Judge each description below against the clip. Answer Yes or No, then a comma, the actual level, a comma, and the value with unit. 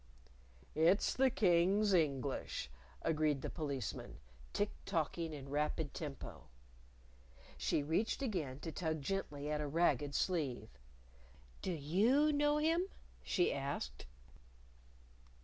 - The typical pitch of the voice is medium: Yes, medium, 160 Hz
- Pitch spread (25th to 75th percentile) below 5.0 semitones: No, average, 5.3 semitones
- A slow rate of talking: Yes, slow, 110 wpm